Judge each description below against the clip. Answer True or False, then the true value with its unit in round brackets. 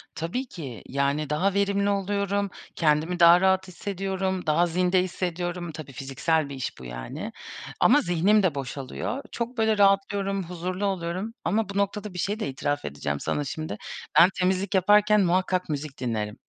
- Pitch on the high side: False (180 Hz)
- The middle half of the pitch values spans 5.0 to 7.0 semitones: False (4.5 semitones)